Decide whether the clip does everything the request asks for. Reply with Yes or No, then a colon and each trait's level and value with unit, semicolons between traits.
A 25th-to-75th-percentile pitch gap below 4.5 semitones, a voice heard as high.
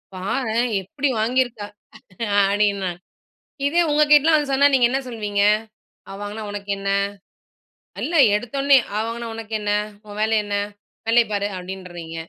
Yes: average, 4.1 semitones; high, 220 Hz